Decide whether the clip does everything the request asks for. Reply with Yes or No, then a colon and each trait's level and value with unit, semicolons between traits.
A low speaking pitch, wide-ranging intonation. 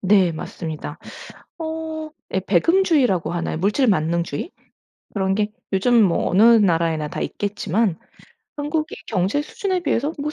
No: high, 205 Hz; wide, 8.9 semitones